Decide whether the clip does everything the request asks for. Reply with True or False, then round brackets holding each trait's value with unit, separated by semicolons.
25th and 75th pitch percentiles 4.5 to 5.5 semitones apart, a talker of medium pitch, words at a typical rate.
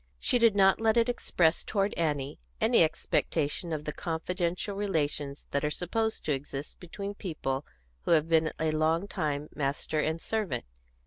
True (4.8 semitones; 160 Hz; 165 wpm)